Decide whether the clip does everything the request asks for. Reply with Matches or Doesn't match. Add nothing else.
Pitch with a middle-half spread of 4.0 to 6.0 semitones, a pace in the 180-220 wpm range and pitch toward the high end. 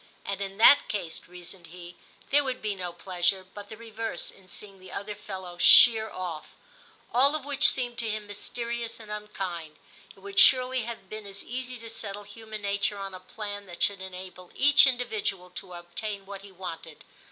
Doesn't match